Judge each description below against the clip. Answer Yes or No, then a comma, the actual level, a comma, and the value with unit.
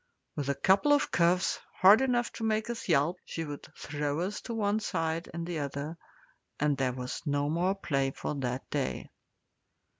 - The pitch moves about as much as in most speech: No, wide, 5.7 semitones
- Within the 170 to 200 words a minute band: Yes, average, 180 wpm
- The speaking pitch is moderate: Yes, medium, 165 Hz